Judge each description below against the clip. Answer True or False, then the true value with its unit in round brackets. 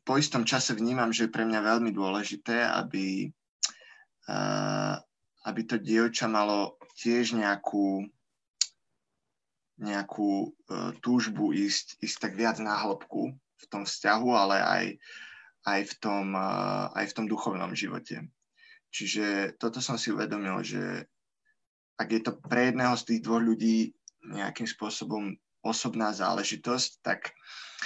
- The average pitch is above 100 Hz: True (110 Hz)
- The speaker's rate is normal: True (125 wpm)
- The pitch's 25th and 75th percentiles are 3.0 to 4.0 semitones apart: False (2.6 semitones)